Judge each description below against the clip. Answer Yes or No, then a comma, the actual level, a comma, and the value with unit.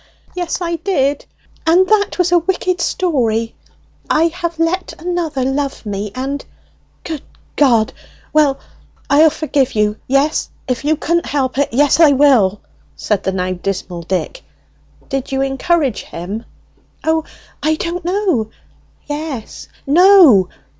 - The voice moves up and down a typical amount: No, wide, 6.0 semitones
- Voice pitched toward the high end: Yes, very high, 290 Hz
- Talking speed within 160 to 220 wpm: No, slow, 135 wpm